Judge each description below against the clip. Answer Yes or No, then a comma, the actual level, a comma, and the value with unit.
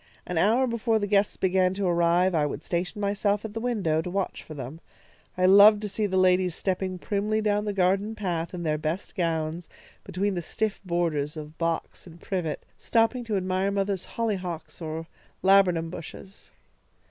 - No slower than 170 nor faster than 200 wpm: Yes, average, 180 wpm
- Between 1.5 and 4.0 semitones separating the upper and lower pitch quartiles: Yes, average, 3.3 semitones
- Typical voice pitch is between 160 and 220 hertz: Yes, medium, 185 Hz